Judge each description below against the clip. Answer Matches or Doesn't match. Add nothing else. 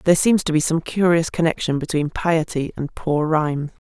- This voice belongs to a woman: Matches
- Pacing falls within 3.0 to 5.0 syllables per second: Doesn't match